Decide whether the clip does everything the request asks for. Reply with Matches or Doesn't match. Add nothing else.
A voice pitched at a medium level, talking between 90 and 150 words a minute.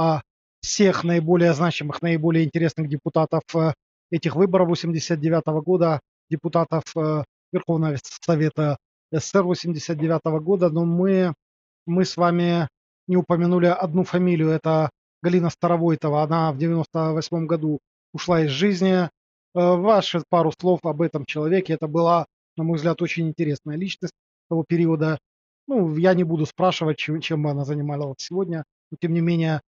Matches